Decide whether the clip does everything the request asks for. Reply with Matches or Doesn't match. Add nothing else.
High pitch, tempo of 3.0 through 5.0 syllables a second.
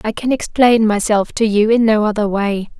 Matches